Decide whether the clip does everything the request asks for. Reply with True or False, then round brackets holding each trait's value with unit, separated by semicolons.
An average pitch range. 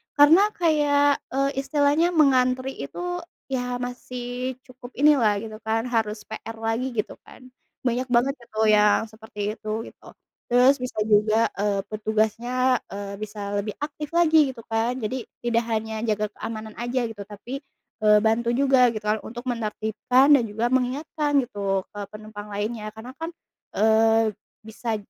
True (3.3 semitones)